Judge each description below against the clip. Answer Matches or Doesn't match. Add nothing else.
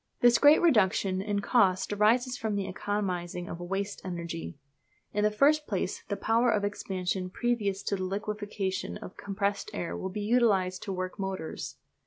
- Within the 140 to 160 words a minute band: Doesn't match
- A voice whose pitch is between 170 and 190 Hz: Doesn't match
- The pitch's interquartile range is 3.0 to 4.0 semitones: Doesn't match